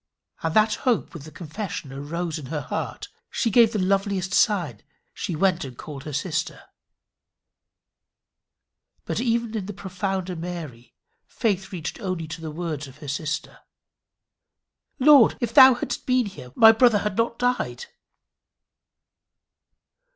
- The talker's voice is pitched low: No, medium, 185 Hz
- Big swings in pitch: Yes, wide, 5.9 semitones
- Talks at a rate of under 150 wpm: Yes, average, 140 wpm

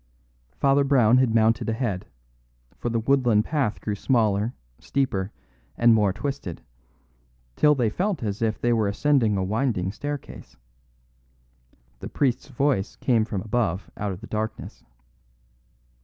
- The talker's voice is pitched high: No, low, 115 Hz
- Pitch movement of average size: Yes, average, 4.4 semitones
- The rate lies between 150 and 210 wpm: No, slow, 135 wpm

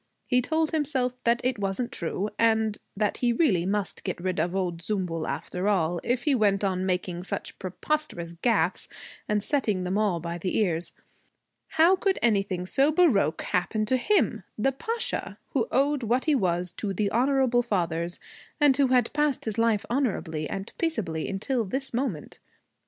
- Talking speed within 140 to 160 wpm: No, average, 170 wpm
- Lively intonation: Yes, wide, 6.2 semitones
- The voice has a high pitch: Yes, high, 215 Hz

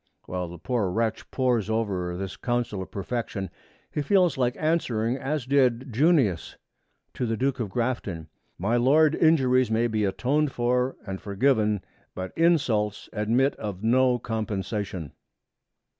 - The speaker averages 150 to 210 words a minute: No, average, 140 wpm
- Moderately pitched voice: No, low, 115 Hz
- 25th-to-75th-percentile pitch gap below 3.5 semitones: No, average, 4.2 semitones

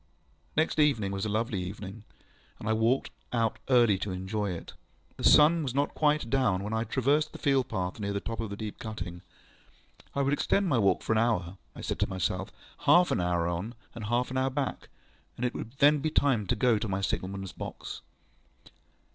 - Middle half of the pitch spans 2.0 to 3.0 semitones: No, average, 5.2 semitones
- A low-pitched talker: Yes, low, 110 Hz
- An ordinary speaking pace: No, fast, 215 wpm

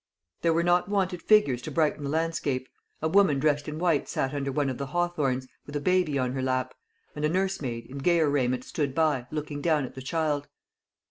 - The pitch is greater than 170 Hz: No, medium, 150 Hz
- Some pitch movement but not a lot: Yes, average, 3.8 semitones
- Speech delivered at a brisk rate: Yes, fast, 210 wpm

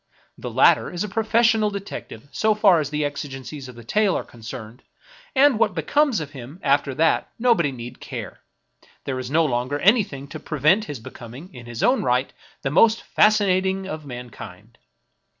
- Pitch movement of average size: No, wide, 8.2 semitones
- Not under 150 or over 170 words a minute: No, average, 180 wpm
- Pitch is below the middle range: No, medium, 150 Hz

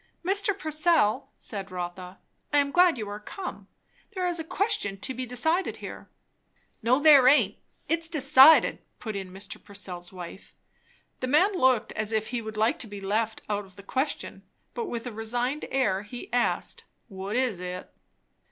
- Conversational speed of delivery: Yes, average, 170 wpm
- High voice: Yes, high, 240 Hz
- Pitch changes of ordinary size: No, wide, 6.7 semitones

